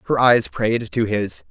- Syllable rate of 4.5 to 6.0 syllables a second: No, 3.9 syllables/s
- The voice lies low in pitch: Yes, low, 110 Hz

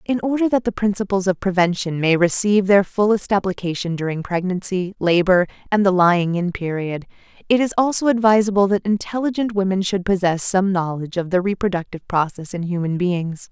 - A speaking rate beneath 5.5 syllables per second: No, 5.7 syllables/s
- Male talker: No, female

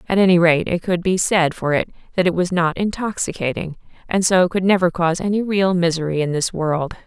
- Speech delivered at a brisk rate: Yes, fast, 210 wpm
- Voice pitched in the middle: Yes, medium, 175 Hz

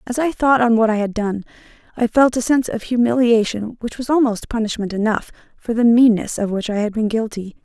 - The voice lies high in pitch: Yes, high, 225 Hz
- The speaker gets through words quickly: Yes, fast, 220 wpm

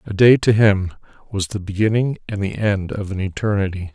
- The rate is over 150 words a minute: Yes, average, 200 wpm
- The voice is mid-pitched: No, low, 100 Hz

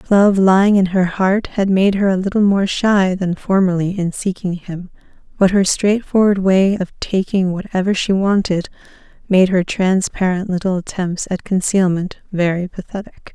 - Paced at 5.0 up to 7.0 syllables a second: No, 4.6 syllables/s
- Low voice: No, high, 190 Hz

